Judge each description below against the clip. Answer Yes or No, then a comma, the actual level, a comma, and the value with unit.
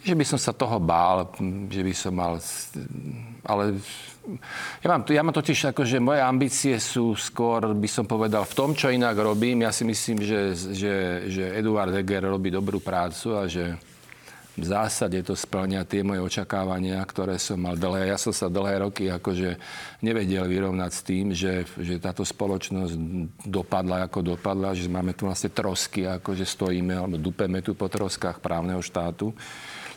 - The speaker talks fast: Yes, fast, 170 wpm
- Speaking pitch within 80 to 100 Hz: Yes, very low, 95 Hz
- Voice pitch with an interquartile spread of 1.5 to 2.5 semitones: No, average, 2.9 semitones